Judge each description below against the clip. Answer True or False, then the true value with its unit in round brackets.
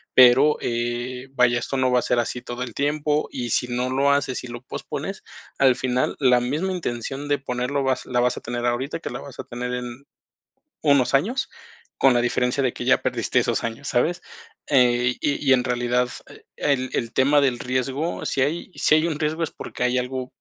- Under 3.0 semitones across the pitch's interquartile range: True (2.4 semitones)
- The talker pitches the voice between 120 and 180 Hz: True (130 Hz)